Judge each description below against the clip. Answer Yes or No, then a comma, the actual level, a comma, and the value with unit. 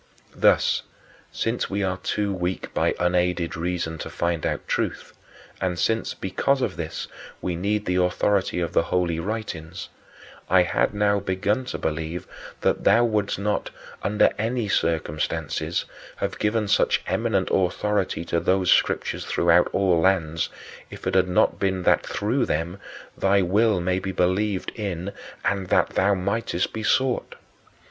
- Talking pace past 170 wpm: No, average, 150 wpm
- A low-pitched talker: Yes, very low, 95 Hz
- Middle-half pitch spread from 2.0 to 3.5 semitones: Yes, average, 2.9 semitones